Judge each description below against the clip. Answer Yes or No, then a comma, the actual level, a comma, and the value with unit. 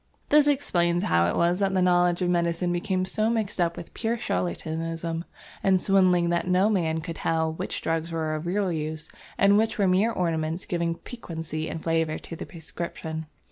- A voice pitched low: No, medium, 170 Hz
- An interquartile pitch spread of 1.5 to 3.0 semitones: Yes, narrow, 2.6 semitones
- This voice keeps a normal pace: Yes, average, 185 wpm